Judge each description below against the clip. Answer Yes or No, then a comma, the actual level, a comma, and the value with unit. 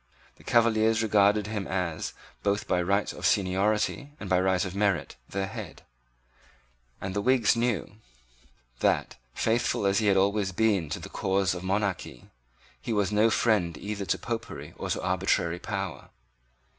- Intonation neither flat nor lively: No, narrow, 2.3 semitones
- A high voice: No, low, 100 Hz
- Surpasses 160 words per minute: No, average, 155 wpm